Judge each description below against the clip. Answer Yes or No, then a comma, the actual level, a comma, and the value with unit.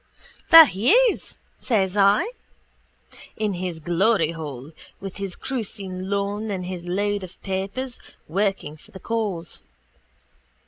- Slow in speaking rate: Yes, slow, 120 wpm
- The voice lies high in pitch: Yes, high, 195 Hz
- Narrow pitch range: No, average, 3.1 semitones